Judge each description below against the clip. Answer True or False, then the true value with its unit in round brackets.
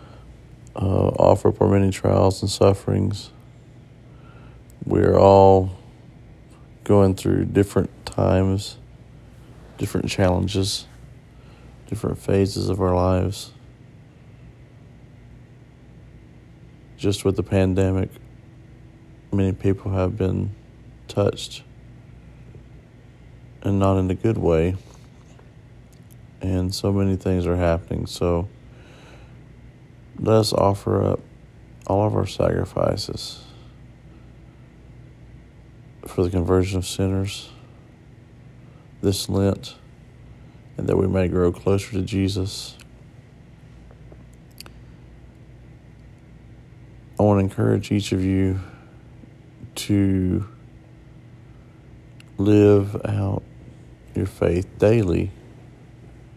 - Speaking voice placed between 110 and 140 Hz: False (100 Hz)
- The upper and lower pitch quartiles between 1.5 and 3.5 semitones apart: False (4.1 semitones)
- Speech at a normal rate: False (85 wpm)